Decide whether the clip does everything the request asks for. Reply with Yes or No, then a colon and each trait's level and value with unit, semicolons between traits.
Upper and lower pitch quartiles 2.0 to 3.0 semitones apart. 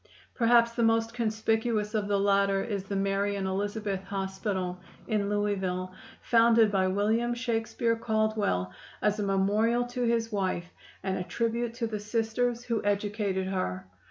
Yes: average, 2.7 semitones